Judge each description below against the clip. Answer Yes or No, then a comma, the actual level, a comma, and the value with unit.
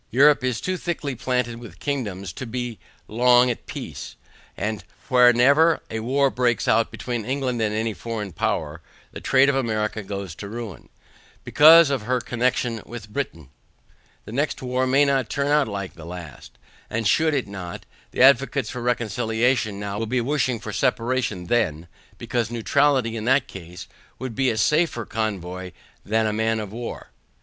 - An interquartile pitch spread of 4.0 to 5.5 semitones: No, average, 3.6 semitones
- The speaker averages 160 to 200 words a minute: Yes, average, 170 wpm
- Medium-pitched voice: No, low, 120 Hz